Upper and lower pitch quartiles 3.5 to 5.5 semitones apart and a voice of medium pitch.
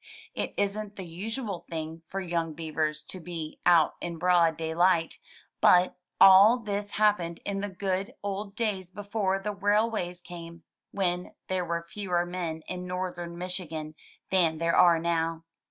No: average, 2.9 semitones; medium, 180 Hz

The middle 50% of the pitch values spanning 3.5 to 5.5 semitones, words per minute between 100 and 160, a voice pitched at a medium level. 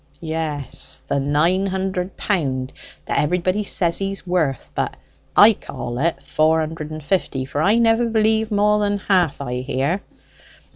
Yes: average, 5.2 semitones; average, 150 wpm; medium, 170 Hz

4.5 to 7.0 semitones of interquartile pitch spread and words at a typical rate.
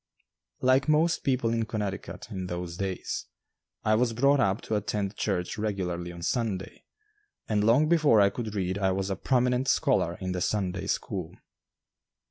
Yes: average, 4.8 semitones; average, 160 wpm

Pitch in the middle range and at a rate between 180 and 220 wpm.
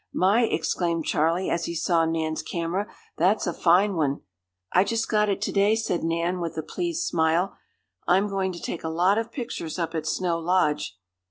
Yes: medium, 175 Hz; average, 190 wpm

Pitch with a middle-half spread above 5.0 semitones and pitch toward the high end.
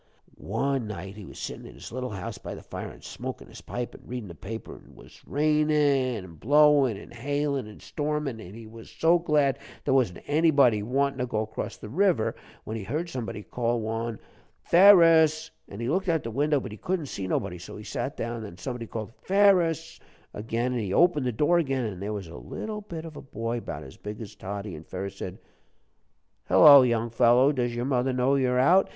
No: wide, 5.4 semitones; low, 125 Hz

